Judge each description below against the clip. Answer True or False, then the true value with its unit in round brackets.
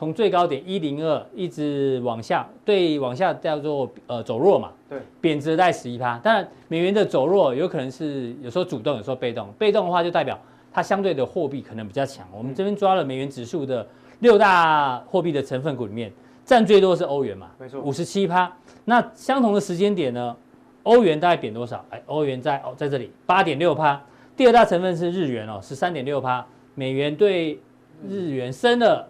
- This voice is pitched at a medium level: True (150 Hz)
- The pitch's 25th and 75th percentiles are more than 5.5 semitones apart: True (6.1 semitones)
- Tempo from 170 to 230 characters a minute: False (300 characters per minute)